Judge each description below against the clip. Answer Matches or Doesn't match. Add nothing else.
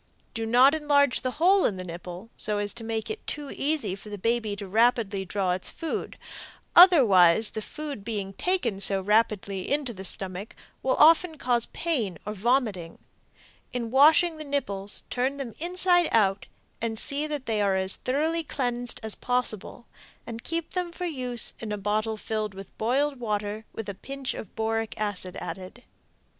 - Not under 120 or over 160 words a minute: Doesn't match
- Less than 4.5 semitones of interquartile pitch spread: Doesn't match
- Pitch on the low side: Doesn't match